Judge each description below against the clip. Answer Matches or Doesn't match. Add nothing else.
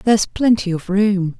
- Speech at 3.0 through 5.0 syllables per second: Matches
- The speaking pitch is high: Matches